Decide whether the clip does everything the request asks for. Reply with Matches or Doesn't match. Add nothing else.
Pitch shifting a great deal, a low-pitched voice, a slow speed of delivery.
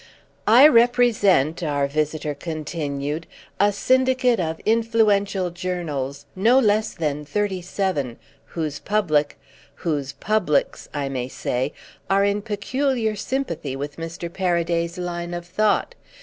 Doesn't match